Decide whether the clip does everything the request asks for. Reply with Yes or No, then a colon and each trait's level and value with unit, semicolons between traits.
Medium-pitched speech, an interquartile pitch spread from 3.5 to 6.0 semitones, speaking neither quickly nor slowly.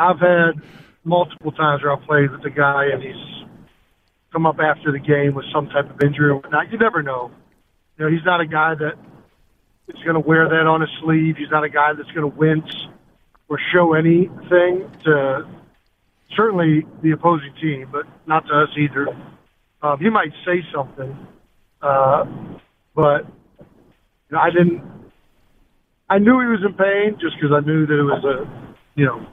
No: medium, 155 Hz; average, 2.8 semitones; average, 180 wpm